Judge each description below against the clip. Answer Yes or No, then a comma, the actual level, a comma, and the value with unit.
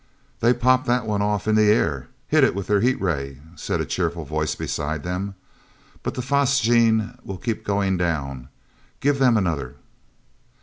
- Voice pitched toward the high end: No, low, 100 Hz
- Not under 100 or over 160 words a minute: No, average, 170 wpm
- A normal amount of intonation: No, wide, 6.4 semitones